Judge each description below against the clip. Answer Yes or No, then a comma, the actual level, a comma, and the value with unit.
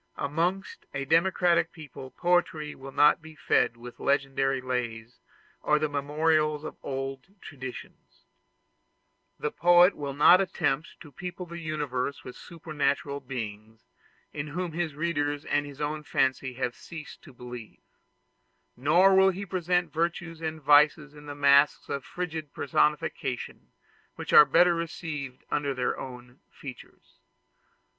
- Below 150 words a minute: Yes, slow, 135 wpm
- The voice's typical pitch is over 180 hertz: No, medium, 150 Hz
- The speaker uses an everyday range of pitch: Yes, average, 3.5 semitones